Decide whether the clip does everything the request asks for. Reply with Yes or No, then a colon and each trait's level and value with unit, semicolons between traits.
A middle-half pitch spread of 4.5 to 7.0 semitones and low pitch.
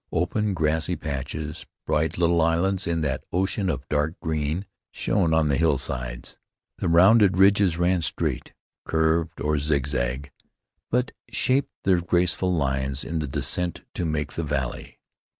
No: average, 3.5 semitones; very low, 80 Hz